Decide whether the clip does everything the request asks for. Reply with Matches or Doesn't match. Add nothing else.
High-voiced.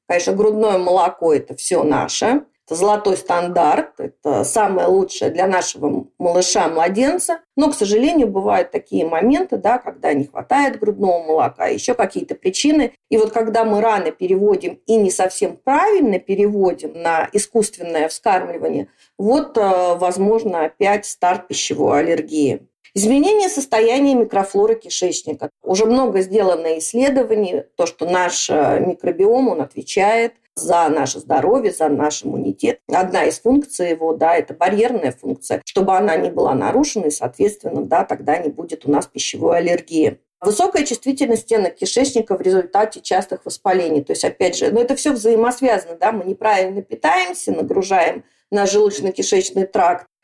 Matches